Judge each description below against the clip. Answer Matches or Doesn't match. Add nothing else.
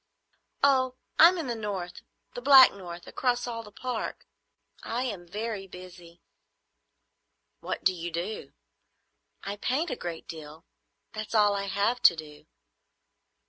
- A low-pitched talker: Doesn't match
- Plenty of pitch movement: Matches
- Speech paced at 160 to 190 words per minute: Doesn't match